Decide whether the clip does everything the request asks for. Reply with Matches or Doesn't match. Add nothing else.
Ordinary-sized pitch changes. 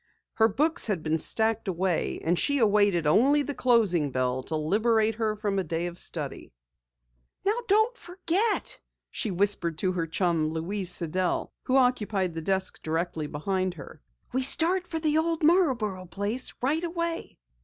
Doesn't match